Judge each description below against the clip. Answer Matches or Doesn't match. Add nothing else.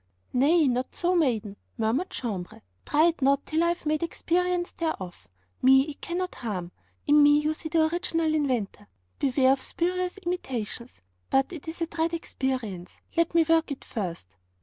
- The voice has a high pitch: Matches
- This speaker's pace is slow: Doesn't match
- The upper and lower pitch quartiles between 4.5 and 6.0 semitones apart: Matches